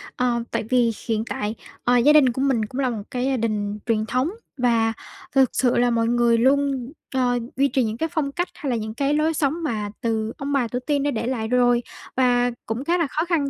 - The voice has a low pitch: No, high, 245 Hz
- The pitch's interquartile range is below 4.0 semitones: Yes, average, 3.3 semitones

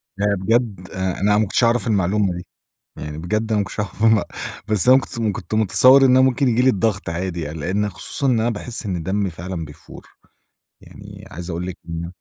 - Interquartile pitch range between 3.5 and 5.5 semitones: Yes, average, 4.2 semitones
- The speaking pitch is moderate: No, low, 100 Hz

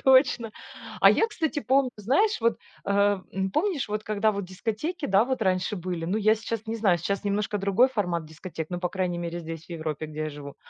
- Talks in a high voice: Yes, high, 200 Hz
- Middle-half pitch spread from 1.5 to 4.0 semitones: No, average, 4.5 semitones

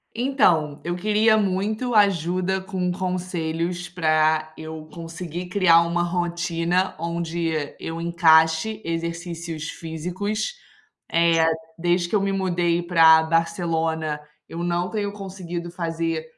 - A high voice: No, medium, 170 Hz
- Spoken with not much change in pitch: Yes, narrow, 2.1 semitones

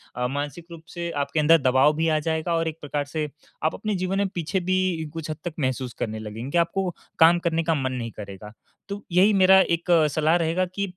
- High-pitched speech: No, medium, 160 Hz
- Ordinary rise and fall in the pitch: Yes, average, 3.7 semitones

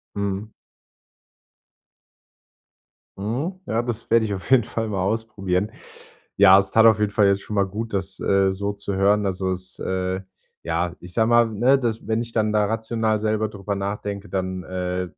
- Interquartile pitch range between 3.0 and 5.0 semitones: No, narrow, 2.6 semitones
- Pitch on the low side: Yes, low, 100 Hz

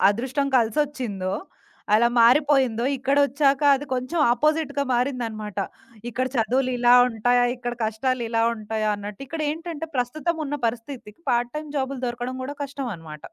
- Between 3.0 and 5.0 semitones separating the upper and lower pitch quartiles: Yes, average, 3.7 semitones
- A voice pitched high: Yes, very high, 250 Hz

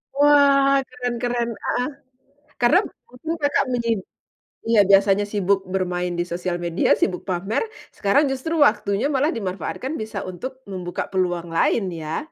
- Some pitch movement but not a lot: No, wide, 6.2 semitones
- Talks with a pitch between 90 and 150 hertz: No, high, 210 Hz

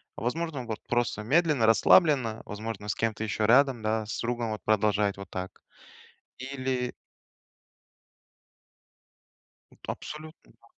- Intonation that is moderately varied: Yes, average, 3.6 semitones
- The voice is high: No, low, 115 Hz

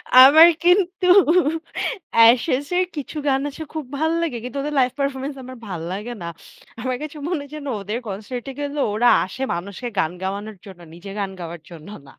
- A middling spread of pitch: No, wide, 6.5 semitones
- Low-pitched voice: No, very high, 255 Hz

